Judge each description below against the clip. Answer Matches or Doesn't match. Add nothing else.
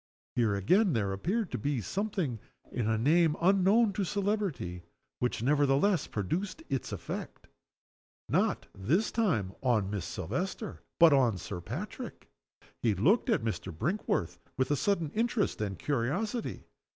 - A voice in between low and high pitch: Matches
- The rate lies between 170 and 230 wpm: Doesn't match